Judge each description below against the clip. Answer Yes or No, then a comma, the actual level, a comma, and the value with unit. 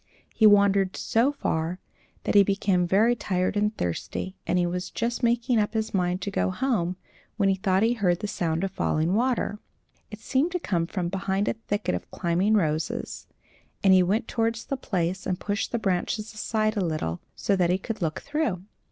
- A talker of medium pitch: No, high, 195 Hz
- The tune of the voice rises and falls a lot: No, average, 3.6 semitones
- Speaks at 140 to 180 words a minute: No, average, 195 wpm